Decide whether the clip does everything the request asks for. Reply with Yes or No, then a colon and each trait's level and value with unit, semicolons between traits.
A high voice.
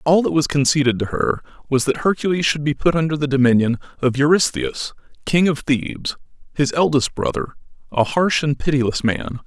No: medium, 145 Hz